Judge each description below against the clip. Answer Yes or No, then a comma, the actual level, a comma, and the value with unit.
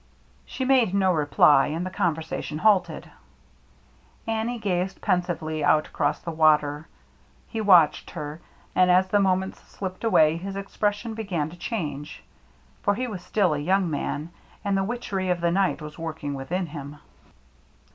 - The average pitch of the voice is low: No, medium, 180 Hz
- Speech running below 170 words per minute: Yes, average, 155 wpm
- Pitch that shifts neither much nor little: Yes, average, 4.2 semitones